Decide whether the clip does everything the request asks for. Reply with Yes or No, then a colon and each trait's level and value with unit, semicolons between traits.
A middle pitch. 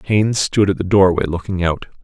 No: very low, 95 Hz